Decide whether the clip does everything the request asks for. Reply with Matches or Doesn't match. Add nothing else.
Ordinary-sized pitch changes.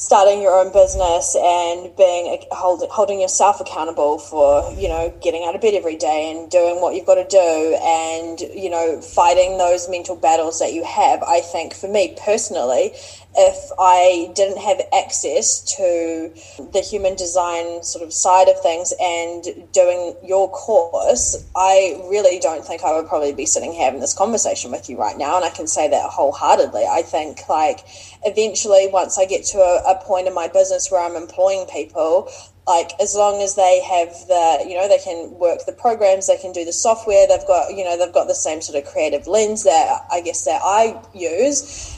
Matches